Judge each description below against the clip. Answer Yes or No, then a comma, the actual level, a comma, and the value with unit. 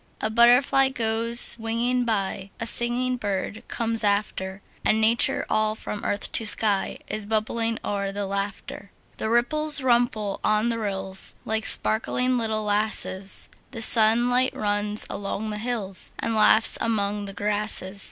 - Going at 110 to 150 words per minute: Yes, average, 140 wpm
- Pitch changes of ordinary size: No, narrow, 2.3 semitones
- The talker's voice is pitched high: Yes, high, 220 Hz